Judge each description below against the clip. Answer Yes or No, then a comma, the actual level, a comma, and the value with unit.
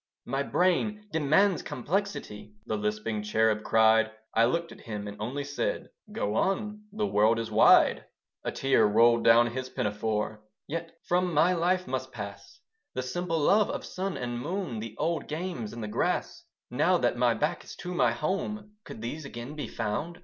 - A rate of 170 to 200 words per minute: Yes, average, 175 wpm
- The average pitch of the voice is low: Yes, low, 130 Hz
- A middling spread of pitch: No, wide, 8.0 semitones